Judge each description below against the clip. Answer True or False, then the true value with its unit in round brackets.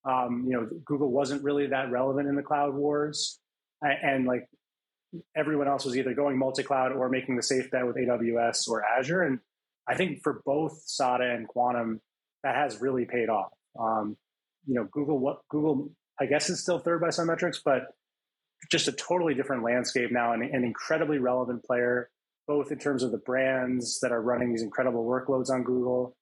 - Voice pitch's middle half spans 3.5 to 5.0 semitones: False (2.7 semitones)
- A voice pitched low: True (130 Hz)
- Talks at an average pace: True (190 wpm)